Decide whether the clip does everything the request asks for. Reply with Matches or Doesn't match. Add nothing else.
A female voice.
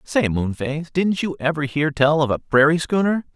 Doesn't match